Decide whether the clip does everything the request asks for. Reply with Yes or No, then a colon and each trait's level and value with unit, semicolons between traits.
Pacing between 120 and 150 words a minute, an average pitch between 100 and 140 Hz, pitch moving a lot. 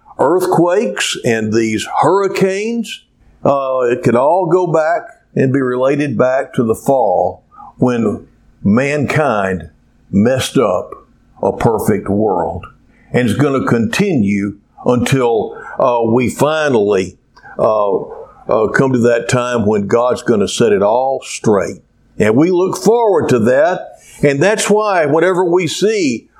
Yes: slow, 135 wpm; low, 135 Hz; wide, 7.3 semitones